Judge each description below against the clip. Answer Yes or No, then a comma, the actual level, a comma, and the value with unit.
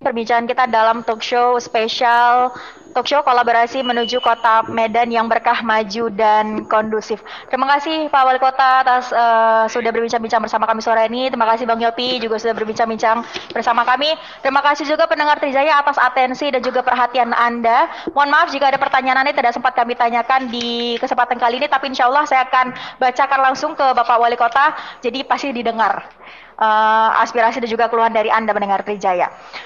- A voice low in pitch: No, high, 245 Hz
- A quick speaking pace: Yes, fast, 175 wpm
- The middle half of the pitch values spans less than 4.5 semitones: Yes, narrow, 2.4 semitones